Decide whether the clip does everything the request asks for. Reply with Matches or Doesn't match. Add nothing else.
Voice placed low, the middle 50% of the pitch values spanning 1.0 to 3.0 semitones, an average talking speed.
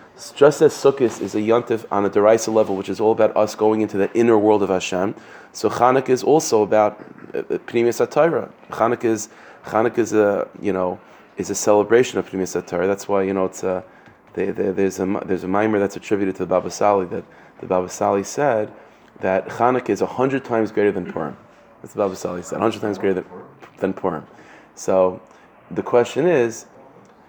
Matches